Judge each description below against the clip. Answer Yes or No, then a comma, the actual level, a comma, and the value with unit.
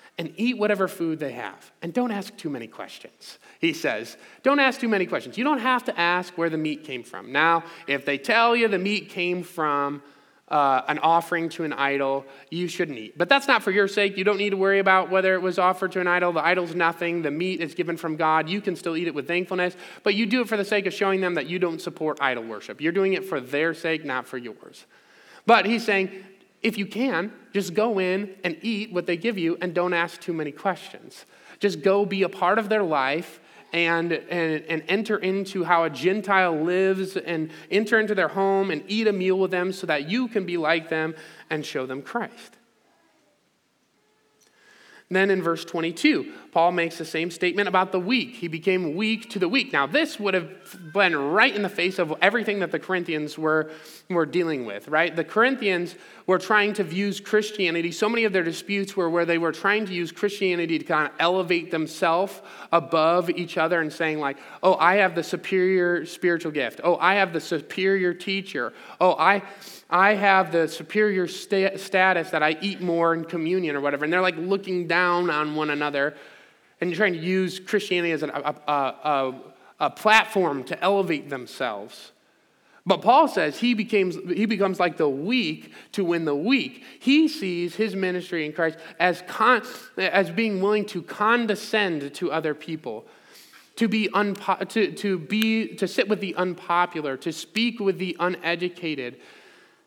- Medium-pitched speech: Yes, medium, 180 Hz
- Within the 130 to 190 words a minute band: No, average, 200 wpm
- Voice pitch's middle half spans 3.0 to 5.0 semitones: Yes, average, 3.5 semitones